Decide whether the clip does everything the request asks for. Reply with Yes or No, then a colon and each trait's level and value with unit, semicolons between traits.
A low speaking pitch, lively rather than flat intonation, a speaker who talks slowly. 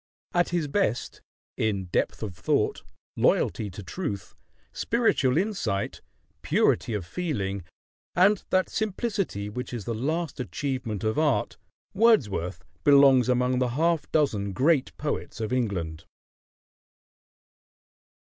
Yes: low, 125 Hz; wide, 8.3 semitones; slow, 115 wpm